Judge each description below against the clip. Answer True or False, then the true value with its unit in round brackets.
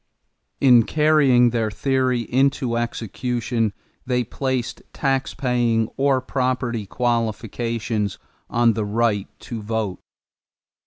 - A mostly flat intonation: True (2.3 semitones)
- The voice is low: True (120 Hz)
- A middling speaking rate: False (95 wpm)